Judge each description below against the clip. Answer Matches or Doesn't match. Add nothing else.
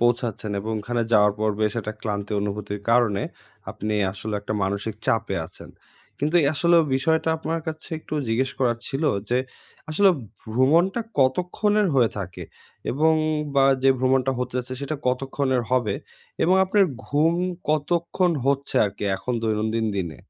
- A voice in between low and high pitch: Doesn't match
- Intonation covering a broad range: Matches